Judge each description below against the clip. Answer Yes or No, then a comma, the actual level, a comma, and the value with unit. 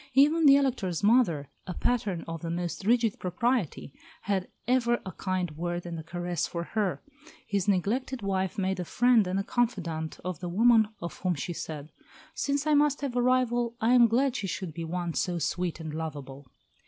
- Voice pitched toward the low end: No, high, 190 Hz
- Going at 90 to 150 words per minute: No, average, 190 wpm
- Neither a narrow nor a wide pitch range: No, wide, 5.9 semitones